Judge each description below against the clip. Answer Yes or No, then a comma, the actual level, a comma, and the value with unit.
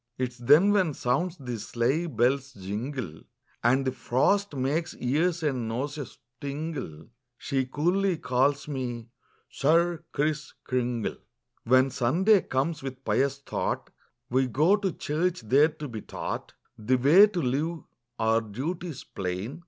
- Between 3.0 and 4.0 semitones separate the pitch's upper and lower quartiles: No, average, 4.7 semitones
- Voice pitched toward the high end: No, low, 135 Hz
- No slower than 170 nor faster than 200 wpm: No, average, 140 wpm